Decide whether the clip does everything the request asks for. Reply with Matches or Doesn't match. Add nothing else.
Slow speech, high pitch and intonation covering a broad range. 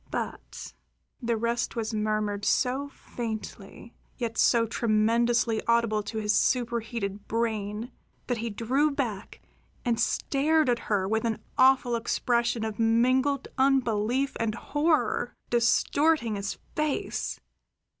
Doesn't match